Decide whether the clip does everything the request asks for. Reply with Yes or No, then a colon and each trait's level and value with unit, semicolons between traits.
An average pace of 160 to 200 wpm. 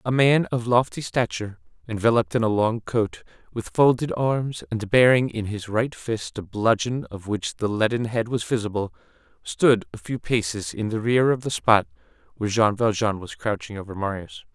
Yes: average, 185 wpm